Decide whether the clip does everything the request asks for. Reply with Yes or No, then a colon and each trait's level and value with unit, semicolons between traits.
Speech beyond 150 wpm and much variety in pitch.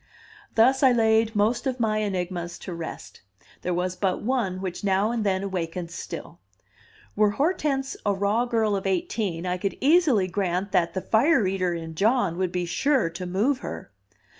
No: average, 175 wpm; average, 4.2 semitones